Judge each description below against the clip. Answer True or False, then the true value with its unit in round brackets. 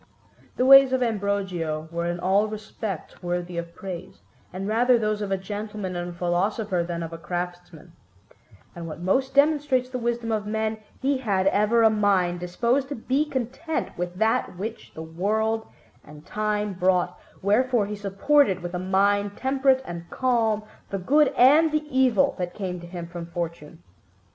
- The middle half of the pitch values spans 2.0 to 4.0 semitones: False (5.0 semitones)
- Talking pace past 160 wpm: True (170 wpm)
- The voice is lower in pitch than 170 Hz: False (205 Hz)